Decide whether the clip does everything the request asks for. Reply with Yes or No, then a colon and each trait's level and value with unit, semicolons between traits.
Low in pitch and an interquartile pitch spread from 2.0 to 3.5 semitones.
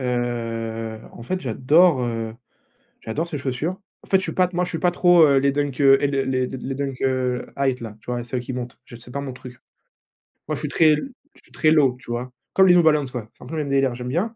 No: low, 130 Hz; average, 4.1 semitones